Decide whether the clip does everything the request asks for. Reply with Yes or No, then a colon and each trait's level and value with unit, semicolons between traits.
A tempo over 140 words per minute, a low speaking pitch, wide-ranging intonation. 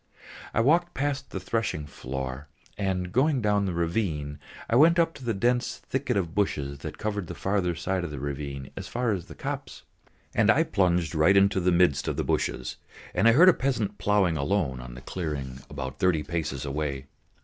Yes: average, 195 wpm; very low, 90 Hz; wide, 7.1 semitones